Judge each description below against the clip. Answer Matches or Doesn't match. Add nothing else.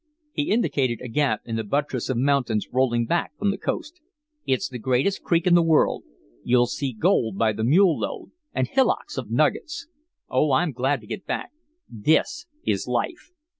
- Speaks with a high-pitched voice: Doesn't match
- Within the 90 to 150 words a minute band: Doesn't match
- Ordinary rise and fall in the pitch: Doesn't match